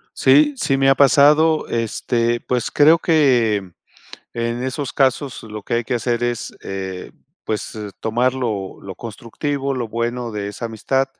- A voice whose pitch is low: Yes, low, 120 Hz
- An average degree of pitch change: Yes, average, 3.4 semitones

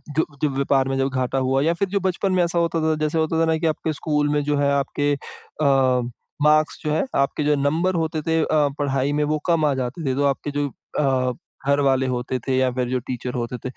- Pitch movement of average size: Yes, average, 3.0 semitones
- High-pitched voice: No, medium, 145 Hz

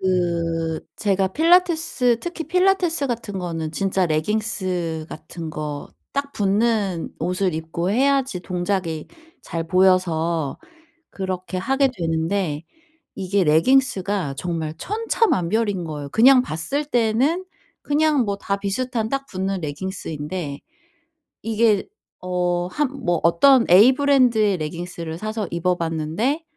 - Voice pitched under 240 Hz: Yes, high, 190 Hz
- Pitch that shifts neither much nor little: No, wide, 6.5 semitones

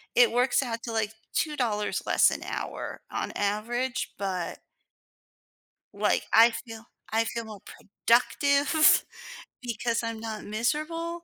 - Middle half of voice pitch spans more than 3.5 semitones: No, average, 2.9 semitones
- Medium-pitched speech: No, high, 230 Hz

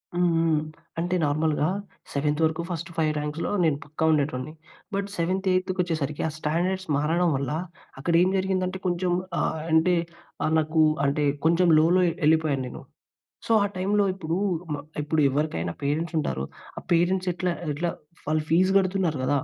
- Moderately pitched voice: Yes, medium, 160 Hz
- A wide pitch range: No, average, 3.2 semitones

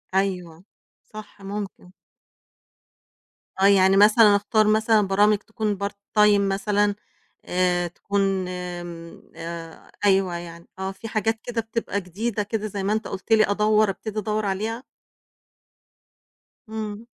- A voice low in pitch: No, high, 200 Hz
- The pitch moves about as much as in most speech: No, narrow, 2.2 semitones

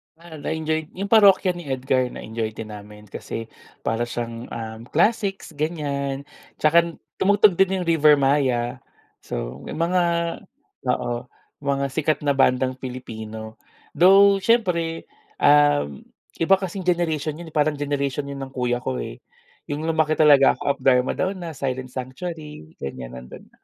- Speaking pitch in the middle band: Yes, medium, 145 Hz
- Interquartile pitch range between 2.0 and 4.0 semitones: No, average, 5.2 semitones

